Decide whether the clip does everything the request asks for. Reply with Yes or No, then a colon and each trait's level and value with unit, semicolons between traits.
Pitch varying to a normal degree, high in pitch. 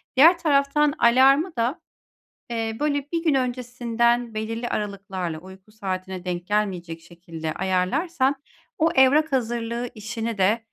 No: wide, 5.9 semitones; high, 230 Hz